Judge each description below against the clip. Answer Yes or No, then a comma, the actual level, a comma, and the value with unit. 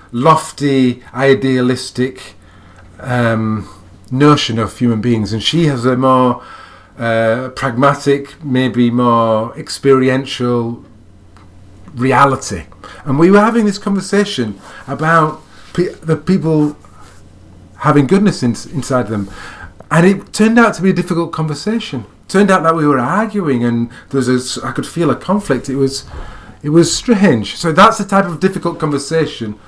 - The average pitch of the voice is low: Yes, low, 130 Hz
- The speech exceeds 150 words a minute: No, average, 140 wpm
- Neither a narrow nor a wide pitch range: No, wide, 6.3 semitones